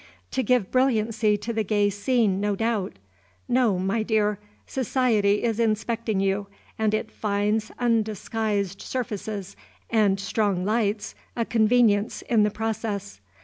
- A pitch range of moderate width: No, narrow, 2.1 semitones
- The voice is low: No, high, 215 Hz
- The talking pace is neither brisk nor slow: No, slow, 130 wpm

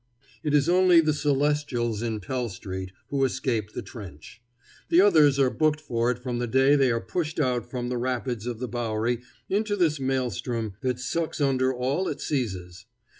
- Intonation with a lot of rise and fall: No, average, 3.8 semitones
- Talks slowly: No, average, 180 wpm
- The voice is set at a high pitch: No, low, 130 Hz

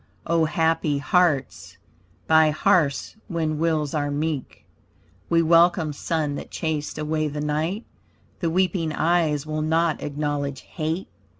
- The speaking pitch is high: No, medium, 155 Hz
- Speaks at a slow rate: Yes, slow, 125 wpm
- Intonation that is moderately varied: No, narrow, 1.9 semitones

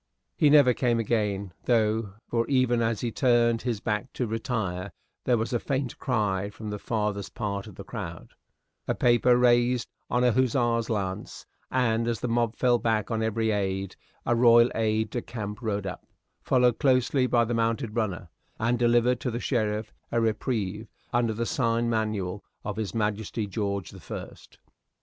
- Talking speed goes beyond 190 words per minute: No, average, 175 wpm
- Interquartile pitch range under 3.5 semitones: Yes, narrow, 2.5 semitones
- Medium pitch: No, low, 115 Hz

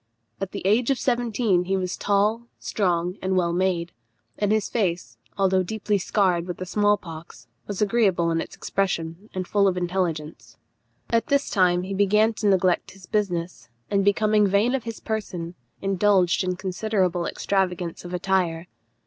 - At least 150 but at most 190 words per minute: Yes, average, 165 wpm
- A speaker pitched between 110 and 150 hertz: No, high, 190 Hz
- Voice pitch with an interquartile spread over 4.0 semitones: No, average, 2.8 semitones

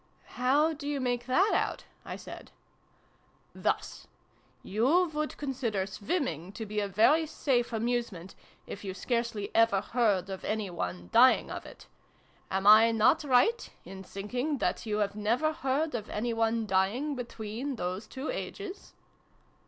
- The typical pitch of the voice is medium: No, high, 230 Hz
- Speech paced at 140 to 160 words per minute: Yes, average, 150 wpm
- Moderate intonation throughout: Yes, average, 4.9 semitones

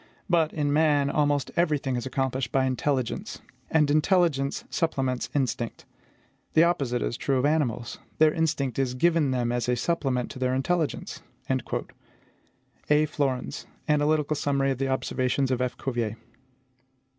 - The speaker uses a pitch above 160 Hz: No, medium, 140 Hz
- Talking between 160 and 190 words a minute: No, average, 140 wpm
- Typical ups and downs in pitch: Yes, average, 3.0 semitones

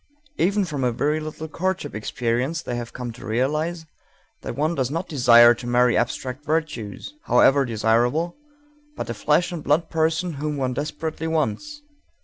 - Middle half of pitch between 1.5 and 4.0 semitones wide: No, average, 4.9 semitones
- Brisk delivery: No, average, 155 wpm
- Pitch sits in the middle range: Yes, medium, 145 Hz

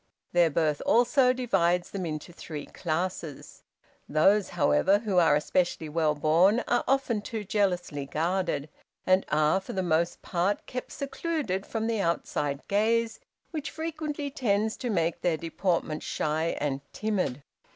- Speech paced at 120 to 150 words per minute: Yes, average, 140 wpm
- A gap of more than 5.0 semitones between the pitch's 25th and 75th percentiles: Yes, wide, 5.6 semitones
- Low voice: No, medium, 185 Hz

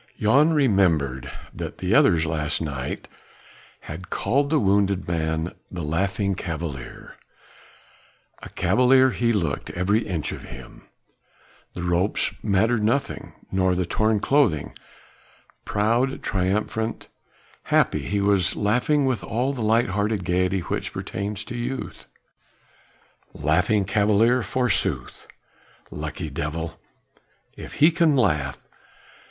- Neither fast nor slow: No, slow, 115 wpm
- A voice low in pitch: Yes, low, 100 Hz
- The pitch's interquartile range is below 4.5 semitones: No, wide, 5.5 semitones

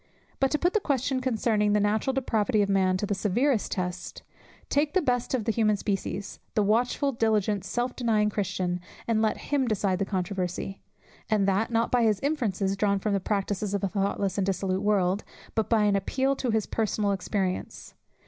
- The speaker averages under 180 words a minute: No, average, 185 wpm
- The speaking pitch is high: Yes, high, 210 Hz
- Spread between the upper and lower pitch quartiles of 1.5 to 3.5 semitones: Yes, average, 3.2 semitones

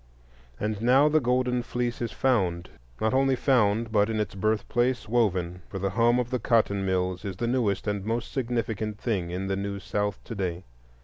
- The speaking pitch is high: No, low, 110 Hz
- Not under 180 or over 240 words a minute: Yes, average, 190 wpm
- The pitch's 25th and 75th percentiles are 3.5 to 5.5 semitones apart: Yes, average, 3.8 semitones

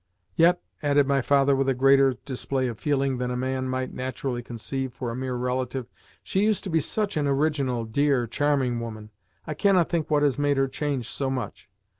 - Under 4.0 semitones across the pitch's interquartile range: Yes, narrow, 2.4 semitones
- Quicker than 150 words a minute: Yes, average, 200 wpm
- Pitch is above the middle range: No, low, 135 Hz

